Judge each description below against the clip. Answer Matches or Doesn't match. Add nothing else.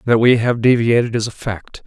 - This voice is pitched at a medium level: Doesn't match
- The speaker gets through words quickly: Matches